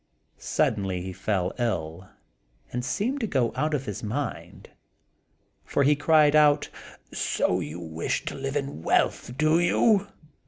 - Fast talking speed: No, average, 145 wpm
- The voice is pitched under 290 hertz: Yes, low, 135 Hz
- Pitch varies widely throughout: Yes, wide, 8.2 semitones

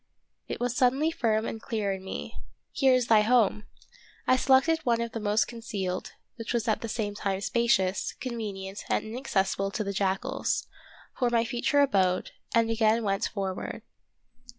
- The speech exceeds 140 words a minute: Yes, average, 170 wpm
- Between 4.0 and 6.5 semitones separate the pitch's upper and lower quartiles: No, average, 3.5 semitones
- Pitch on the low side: No, high, 225 Hz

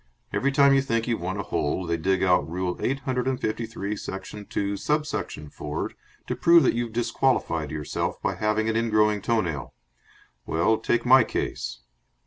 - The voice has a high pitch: No, low, 110 Hz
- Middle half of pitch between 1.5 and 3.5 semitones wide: No, wide, 5.5 semitones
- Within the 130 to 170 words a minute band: No, average, 185 wpm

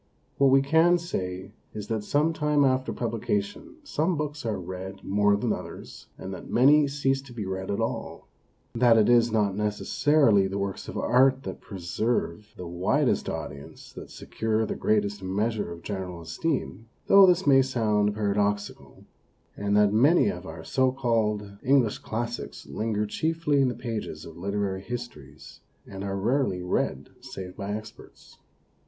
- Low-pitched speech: Yes, low, 110 Hz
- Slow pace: No, average, 160 wpm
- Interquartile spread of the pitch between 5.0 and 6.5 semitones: Yes, average, 5.3 semitones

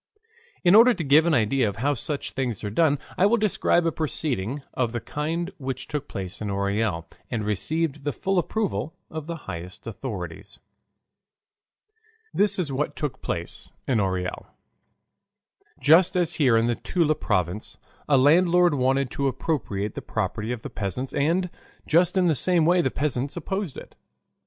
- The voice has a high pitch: No, medium, 140 Hz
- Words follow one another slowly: No, average, 165 wpm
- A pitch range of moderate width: No, wide, 6.9 semitones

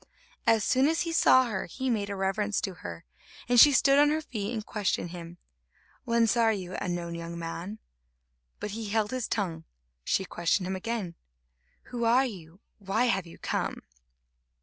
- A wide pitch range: No, average, 4.7 semitones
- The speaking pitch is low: No, high, 210 Hz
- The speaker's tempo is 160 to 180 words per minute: Yes, average, 175 wpm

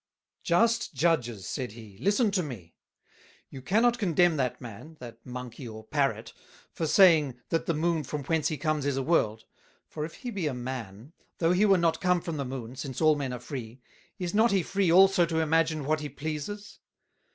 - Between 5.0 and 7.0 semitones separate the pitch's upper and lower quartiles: Yes, wide, 5.4 semitones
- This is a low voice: No, medium, 155 Hz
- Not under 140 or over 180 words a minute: No, average, 195 wpm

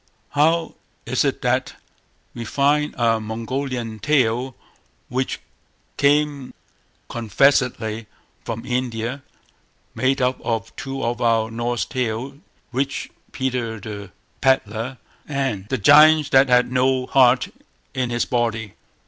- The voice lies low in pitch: Yes, low, 125 Hz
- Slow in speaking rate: Yes, slow, 115 wpm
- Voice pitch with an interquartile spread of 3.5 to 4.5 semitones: No, average, 3.0 semitones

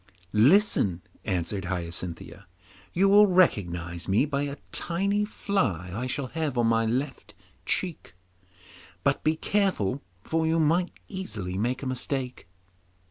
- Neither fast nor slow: No, slow, 130 wpm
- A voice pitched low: Yes, low, 130 Hz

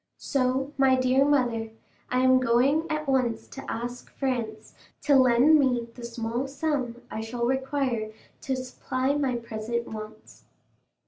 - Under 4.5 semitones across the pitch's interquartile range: Yes, narrow, 2.4 semitones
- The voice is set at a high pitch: Yes, very high, 255 Hz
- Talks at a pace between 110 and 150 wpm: Yes, average, 140 wpm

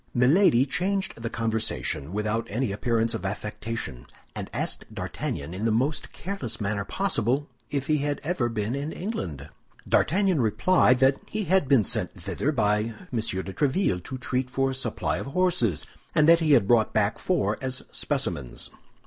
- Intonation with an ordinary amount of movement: No, wide, 5.7 semitones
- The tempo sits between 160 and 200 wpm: Yes, average, 165 wpm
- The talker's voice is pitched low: Yes, low, 125 Hz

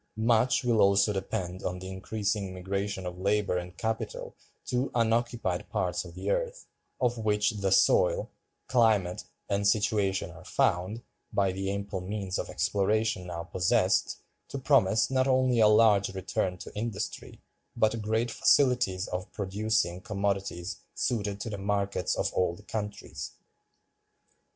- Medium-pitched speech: No, low, 105 Hz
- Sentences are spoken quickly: No, average, 140 wpm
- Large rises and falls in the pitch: No, average, 3.0 semitones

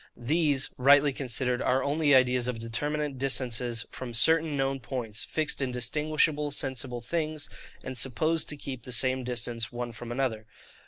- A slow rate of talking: No, average, 155 wpm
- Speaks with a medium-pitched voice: No, low, 130 Hz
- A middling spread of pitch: Yes, average, 3.2 semitones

